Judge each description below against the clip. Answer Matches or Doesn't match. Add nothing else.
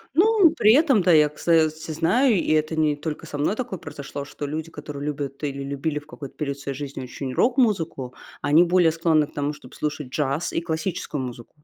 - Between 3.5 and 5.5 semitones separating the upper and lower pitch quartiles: Doesn't match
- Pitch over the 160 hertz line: Doesn't match